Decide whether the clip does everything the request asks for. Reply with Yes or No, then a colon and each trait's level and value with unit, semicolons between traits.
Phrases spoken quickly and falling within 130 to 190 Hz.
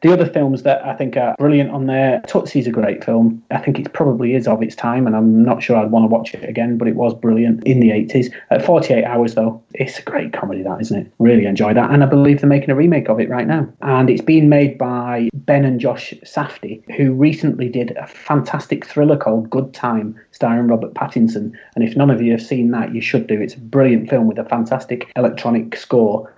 No: fast, 240 wpm; low, 120 Hz